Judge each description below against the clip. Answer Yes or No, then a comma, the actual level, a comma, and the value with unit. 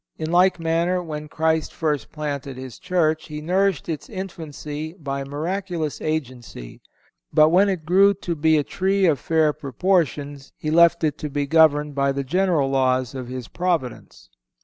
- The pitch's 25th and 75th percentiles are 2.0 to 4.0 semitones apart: Yes, average, 3.6 semitones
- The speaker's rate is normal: Yes, average, 165 wpm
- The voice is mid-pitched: Yes, medium, 155 Hz